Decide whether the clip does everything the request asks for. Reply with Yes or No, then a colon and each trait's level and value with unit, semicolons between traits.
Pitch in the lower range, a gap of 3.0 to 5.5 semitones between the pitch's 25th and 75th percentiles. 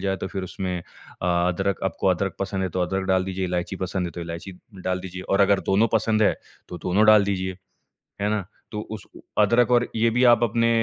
No: very low, 95 Hz; narrow, 2.4 semitones